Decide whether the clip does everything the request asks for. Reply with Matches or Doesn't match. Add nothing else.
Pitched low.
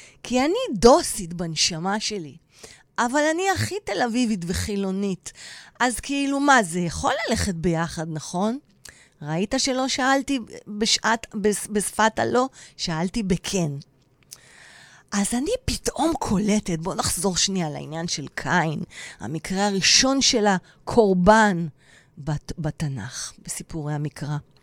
Doesn't match